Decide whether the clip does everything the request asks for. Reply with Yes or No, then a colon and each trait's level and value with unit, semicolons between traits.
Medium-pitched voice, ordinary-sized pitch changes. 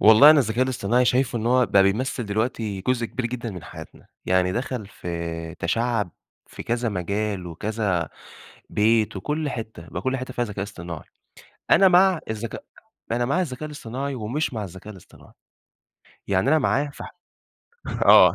No: low, 115 Hz; average, 4.6 semitones